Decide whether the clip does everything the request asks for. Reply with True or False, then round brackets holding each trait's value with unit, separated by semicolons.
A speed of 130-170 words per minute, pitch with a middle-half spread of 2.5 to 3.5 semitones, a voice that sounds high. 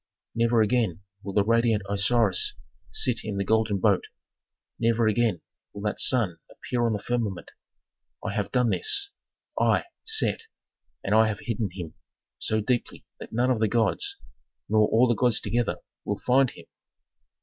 False (160 wpm; 2.8 semitones; 110 Hz)